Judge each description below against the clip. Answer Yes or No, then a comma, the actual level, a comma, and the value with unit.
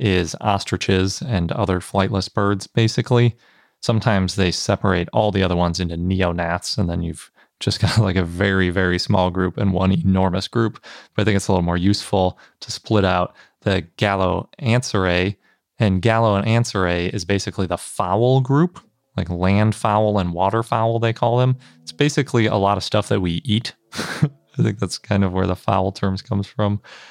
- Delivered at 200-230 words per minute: No, average, 180 wpm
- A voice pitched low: Yes, low, 100 Hz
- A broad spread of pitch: No, average, 3.0 semitones